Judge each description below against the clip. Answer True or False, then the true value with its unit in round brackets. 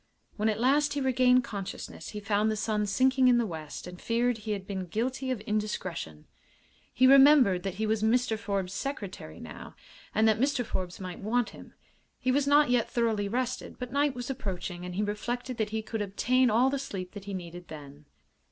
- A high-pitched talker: True (220 Hz)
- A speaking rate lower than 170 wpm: False (200 wpm)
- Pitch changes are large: False (4.4 semitones)